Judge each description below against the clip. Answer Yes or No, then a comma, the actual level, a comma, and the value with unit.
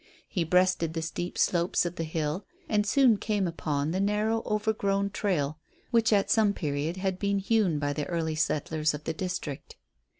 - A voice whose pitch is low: No, medium, 180 Hz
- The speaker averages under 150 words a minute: No, average, 175 wpm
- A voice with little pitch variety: No, average, 4.5 semitones